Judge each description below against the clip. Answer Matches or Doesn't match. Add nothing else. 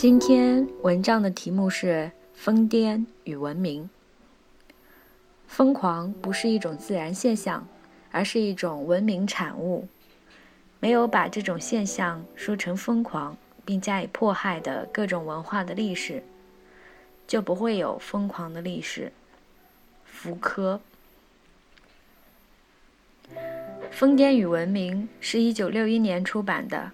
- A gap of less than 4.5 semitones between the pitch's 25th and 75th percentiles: Matches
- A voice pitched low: Doesn't match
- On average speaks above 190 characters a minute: Doesn't match